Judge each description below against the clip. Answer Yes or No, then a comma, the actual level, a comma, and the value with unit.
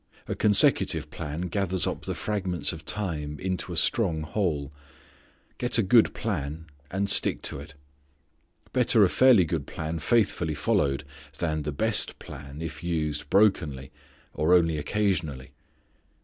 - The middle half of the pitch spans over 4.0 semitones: Yes, average, 4.8 semitones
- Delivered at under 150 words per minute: Yes, average, 140 wpm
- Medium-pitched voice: No, very low, 85 Hz